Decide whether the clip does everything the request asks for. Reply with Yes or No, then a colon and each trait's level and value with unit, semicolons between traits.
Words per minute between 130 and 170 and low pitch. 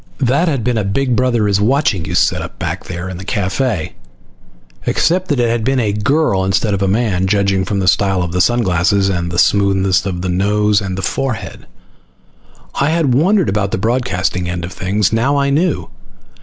No: average, 195 wpm; low, 105 Hz